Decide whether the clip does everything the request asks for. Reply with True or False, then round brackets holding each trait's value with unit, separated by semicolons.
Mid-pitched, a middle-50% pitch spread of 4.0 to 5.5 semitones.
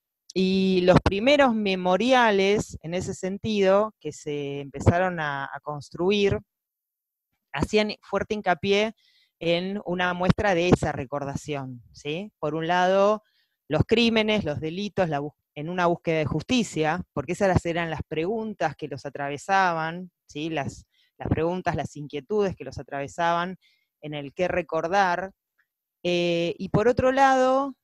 True (180 Hz; 4.8 semitones)